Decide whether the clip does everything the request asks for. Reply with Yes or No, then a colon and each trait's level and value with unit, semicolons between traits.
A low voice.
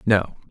Yes: low, 105 Hz